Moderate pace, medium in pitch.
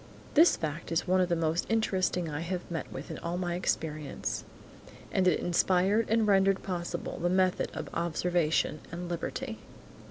Yes: average, 165 wpm; medium, 175 Hz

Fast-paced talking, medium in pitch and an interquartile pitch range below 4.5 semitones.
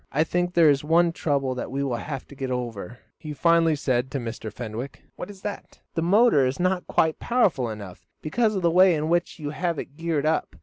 No: fast, 225 wpm; medium, 150 Hz; average, 4.8 semitones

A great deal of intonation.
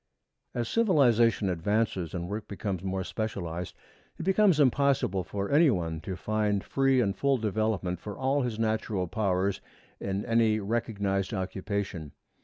No: average, 3.7 semitones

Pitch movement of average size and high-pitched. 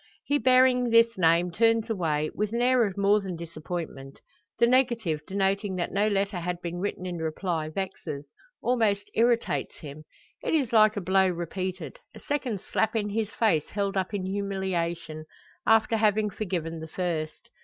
Yes: average, 4.5 semitones; high, 195 Hz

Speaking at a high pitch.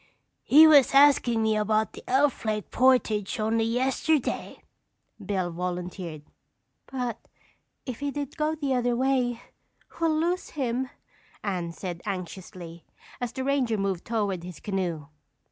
Yes: high, 230 Hz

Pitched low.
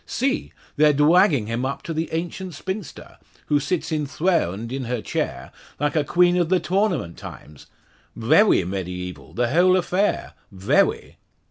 No: medium, 150 Hz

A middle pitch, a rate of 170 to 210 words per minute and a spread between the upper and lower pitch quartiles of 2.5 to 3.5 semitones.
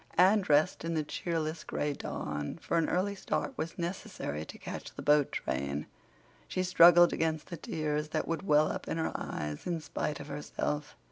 Yes: medium, 155 Hz; average, 185 wpm; average, 2.8 semitones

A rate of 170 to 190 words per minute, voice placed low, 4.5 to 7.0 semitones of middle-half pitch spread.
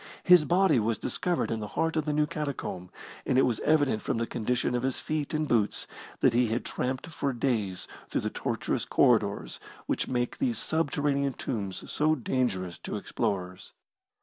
Yes: average, 175 wpm; low, 130 Hz; average, 5.2 semitones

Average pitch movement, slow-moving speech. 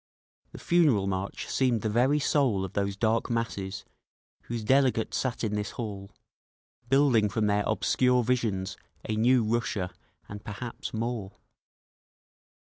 Yes: average, 3.6 semitones; slow, 130 wpm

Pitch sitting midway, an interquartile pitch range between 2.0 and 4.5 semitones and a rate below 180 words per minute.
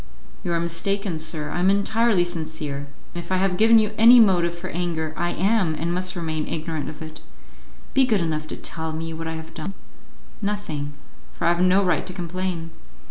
No: medium, 175 Hz; average, 3.2 semitones; average, 200 wpm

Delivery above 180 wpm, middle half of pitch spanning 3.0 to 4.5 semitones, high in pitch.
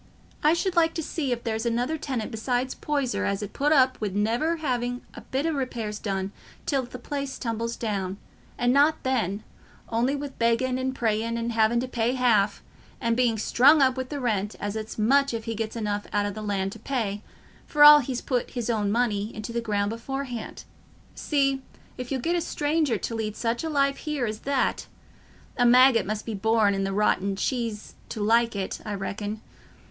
Yes: average, 195 wpm; average, 3.8 semitones; high, 235 Hz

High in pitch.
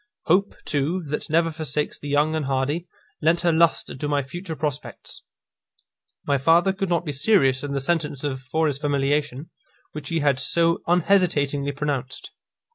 No: medium, 150 Hz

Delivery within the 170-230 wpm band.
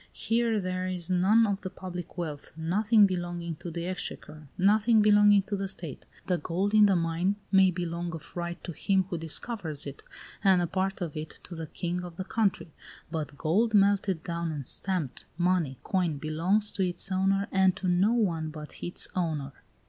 Yes: average, 185 wpm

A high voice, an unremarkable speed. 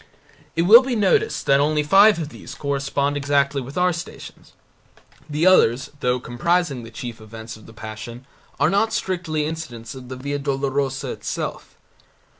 No: medium, 140 Hz; average, 160 wpm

